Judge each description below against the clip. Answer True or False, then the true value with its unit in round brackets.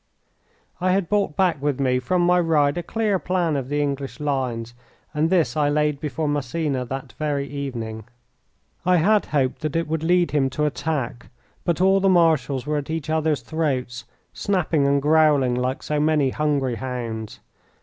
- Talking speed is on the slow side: False (175 wpm)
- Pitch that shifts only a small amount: False (3.5 semitones)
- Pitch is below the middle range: False (150 Hz)